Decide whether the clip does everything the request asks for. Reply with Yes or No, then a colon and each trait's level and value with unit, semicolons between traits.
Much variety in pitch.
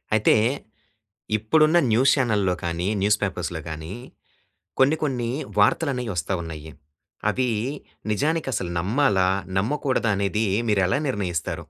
Yes: wide, 6.5 semitones